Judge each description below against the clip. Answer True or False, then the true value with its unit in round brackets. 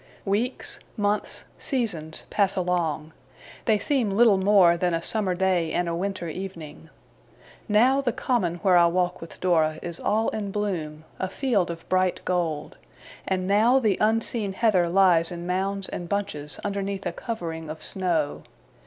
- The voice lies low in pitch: False (185 Hz)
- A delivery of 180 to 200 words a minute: False (155 wpm)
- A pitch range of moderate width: True (3.3 semitones)